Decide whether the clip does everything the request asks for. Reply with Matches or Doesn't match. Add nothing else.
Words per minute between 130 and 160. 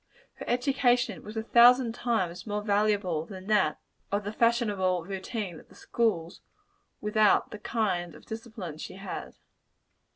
Matches